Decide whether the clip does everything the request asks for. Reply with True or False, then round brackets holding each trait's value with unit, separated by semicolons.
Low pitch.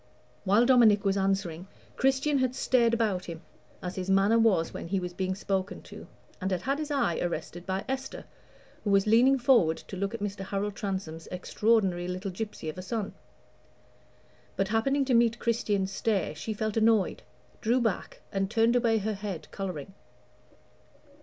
False (205 Hz)